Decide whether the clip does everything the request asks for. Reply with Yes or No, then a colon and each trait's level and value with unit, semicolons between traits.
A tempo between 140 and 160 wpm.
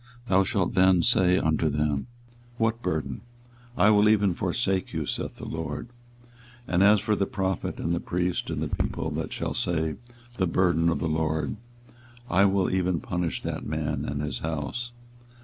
No: average, 175 wpm